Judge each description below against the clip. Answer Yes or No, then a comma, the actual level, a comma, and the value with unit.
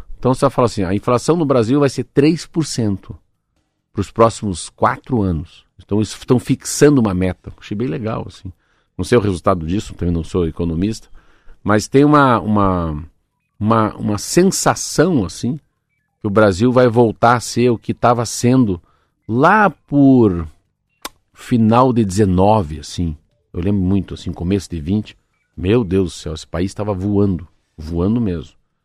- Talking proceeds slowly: No, average, 160 wpm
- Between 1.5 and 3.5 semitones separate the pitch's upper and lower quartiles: No, average, 4.8 semitones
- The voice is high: No, low, 105 Hz